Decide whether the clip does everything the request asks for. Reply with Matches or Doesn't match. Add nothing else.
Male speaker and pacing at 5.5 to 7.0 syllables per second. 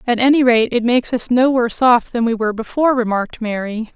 Doesn't match